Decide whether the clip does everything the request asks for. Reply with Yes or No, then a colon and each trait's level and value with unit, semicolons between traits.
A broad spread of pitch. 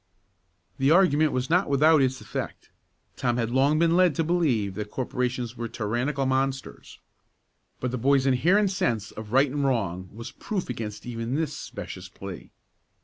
No: average, 4.3 semitones